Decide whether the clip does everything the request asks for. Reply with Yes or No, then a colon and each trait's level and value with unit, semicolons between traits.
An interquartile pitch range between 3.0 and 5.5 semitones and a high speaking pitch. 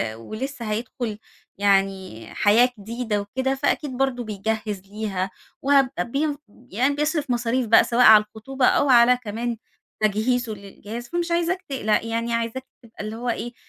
Yes: average, 3.5 semitones; high, 230 Hz